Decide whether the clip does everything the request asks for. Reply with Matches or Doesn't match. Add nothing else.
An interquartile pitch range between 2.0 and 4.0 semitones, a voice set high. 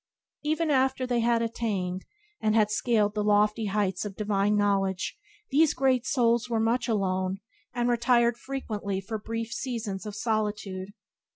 Matches